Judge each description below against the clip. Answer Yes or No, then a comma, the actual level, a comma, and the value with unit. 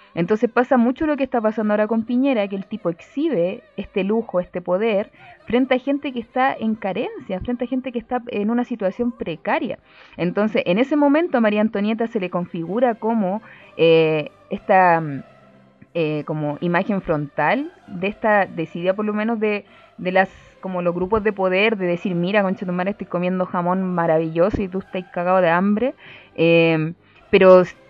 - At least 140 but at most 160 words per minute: No, average, 175 wpm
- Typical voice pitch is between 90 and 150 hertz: No, high, 200 Hz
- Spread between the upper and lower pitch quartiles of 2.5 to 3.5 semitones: No, average, 4.8 semitones